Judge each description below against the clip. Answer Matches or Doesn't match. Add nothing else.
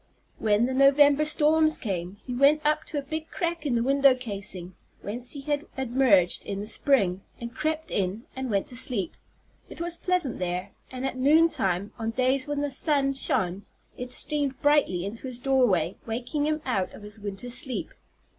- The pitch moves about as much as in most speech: Doesn't match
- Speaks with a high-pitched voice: Matches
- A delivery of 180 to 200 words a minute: Matches